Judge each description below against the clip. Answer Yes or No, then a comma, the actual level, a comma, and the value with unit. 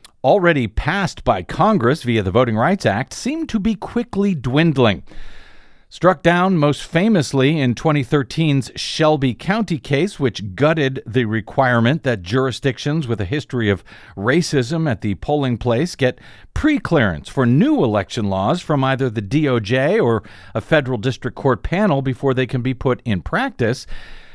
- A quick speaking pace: No, average, 150 wpm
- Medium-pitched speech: No, low, 130 Hz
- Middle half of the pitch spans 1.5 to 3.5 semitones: No, average, 5.1 semitones